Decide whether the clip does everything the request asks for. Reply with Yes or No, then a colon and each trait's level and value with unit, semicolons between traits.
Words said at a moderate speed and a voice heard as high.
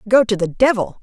No: fast, 235 wpm; high, 220 Hz